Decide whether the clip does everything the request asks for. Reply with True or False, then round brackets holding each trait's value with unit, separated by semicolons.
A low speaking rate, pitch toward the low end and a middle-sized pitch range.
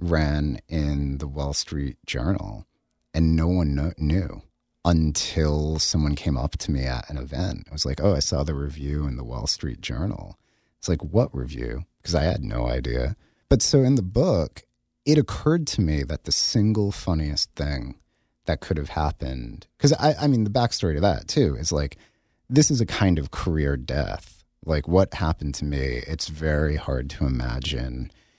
False (185 wpm; 75 Hz; 4.4 semitones)